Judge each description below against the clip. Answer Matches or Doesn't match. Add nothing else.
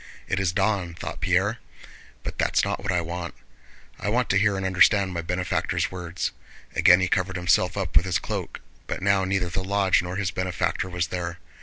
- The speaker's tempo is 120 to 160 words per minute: Doesn't match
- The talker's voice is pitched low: Matches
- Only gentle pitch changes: Matches